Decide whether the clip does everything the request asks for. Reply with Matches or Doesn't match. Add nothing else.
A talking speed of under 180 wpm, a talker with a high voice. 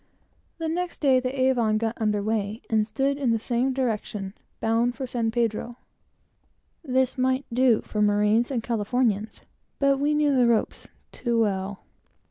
Matches